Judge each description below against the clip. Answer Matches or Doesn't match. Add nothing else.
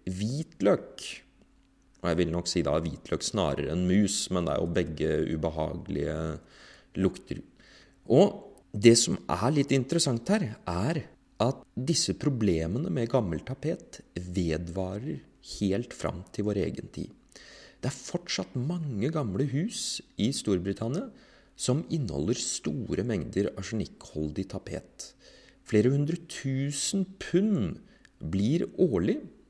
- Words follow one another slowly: Matches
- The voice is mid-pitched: Doesn't match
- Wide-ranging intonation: Matches